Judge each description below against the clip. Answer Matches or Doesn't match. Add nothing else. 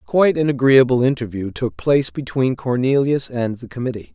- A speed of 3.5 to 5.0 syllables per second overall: Doesn't match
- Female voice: Doesn't match